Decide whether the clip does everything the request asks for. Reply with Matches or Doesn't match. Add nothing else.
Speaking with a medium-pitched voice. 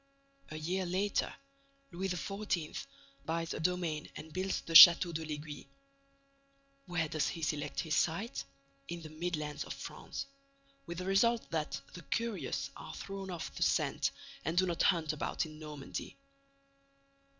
Matches